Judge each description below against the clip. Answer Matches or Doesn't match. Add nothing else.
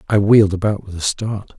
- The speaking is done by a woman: Doesn't match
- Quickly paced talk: Matches